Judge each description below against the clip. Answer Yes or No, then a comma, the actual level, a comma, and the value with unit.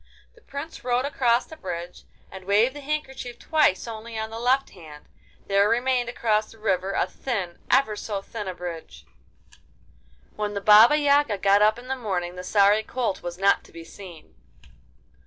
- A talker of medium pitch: No, high, 215 Hz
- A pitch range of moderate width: Yes, average, 4.5 semitones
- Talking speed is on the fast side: No, average, 175 wpm